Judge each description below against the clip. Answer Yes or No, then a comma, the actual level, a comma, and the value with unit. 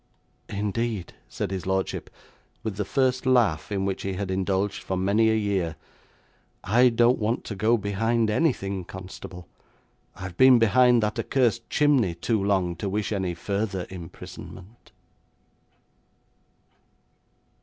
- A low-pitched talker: Yes, low, 100 Hz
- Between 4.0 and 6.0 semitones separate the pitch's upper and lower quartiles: No, average, 3.5 semitones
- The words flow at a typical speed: No, slow, 130 wpm